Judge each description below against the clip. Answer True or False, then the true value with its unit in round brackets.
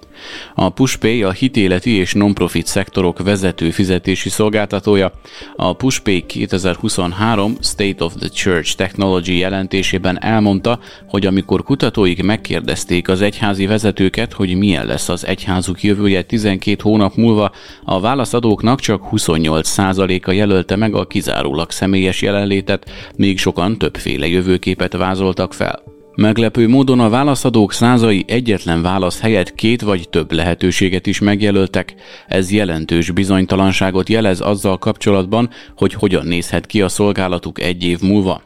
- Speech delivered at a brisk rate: False (130 wpm)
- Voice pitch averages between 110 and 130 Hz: False (95 Hz)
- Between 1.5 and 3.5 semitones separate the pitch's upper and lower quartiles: True (2.5 semitones)